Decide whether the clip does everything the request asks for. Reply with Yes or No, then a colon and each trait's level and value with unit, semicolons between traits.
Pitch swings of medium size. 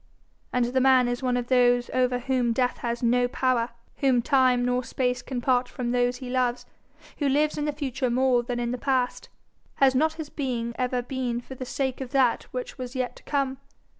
No: narrow, 1.3 semitones